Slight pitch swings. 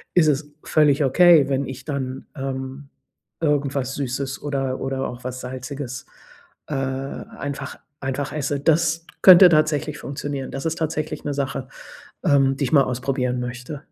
Yes: narrow, 2.0 semitones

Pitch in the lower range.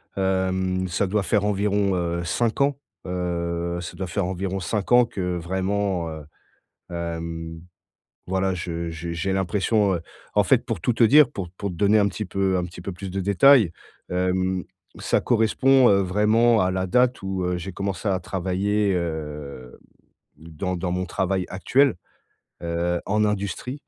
Yes: very low, 95 Hz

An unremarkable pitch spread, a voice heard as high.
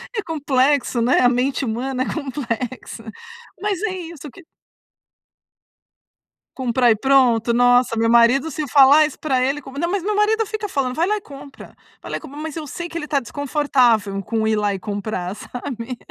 Yes: average, 4.7 semitones; very high, 270 Hz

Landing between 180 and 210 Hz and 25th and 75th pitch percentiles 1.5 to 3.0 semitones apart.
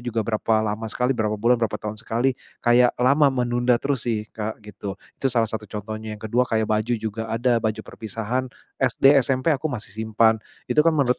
No: low, 115 Hz; narrow, 2.4 semitones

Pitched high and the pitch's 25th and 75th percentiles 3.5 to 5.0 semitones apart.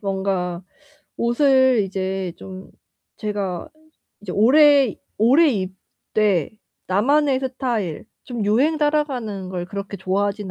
No: high, 210 Hz; wide, 5.5 semitones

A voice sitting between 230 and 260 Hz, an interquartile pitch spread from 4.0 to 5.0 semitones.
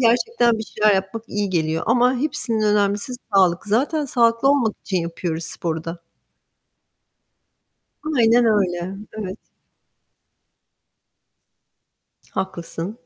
No: high, 210 Hz; average, 4.6 semitones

